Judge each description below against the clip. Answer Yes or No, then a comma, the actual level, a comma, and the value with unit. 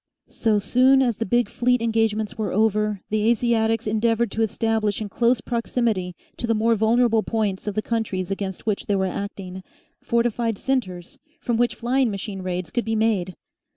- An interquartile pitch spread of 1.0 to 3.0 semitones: Yes, narrow, 2.6 semitones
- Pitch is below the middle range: No, high, 220 Hz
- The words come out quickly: No, average, 175 wpm